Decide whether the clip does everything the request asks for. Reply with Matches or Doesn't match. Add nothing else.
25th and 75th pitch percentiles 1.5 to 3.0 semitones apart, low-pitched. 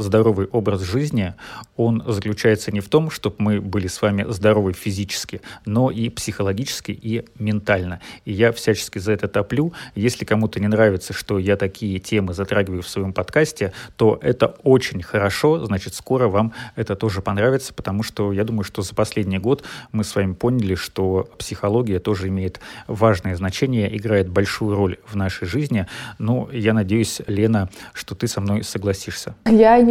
Matches